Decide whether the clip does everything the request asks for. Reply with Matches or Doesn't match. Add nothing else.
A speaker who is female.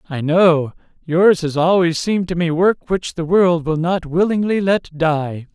Doesn't match